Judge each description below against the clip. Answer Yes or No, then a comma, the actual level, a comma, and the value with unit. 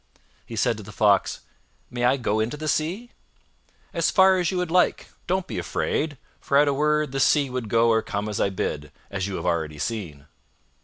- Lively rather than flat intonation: Yes, wide, 7.2 semitones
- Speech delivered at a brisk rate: Yes, fast, 210 wpm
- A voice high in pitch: No, low, 130 Hz